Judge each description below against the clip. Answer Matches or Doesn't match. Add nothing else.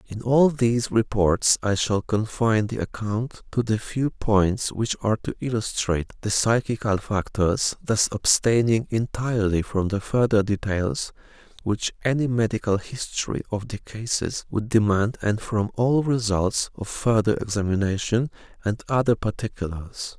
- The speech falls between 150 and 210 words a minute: Doesn't match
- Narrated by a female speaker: Doesn't match